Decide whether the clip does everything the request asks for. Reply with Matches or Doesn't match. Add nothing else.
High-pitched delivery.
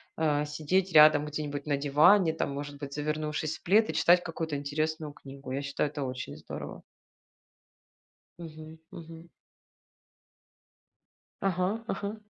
Doesn't match